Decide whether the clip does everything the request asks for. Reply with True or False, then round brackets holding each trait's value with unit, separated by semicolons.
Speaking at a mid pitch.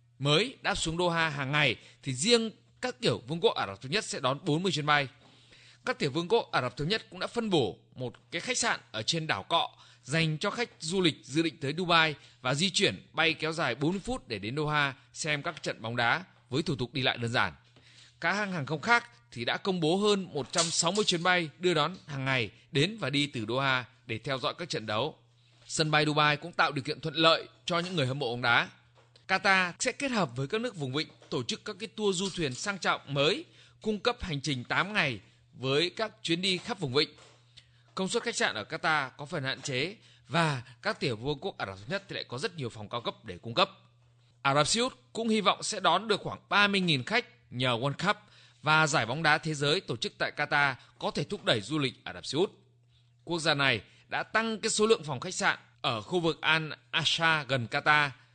True (150 Hz)